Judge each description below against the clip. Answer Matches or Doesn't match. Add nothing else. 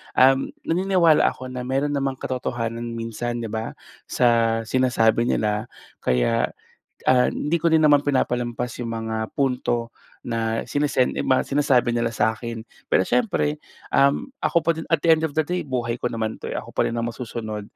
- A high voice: Doesn't match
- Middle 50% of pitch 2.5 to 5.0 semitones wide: Matches